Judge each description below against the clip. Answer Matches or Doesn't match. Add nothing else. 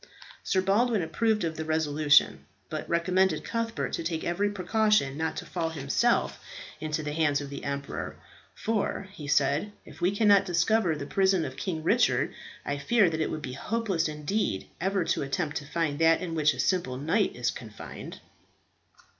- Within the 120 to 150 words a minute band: Doesn't match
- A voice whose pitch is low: Doesn't match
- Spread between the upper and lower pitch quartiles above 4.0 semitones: Matches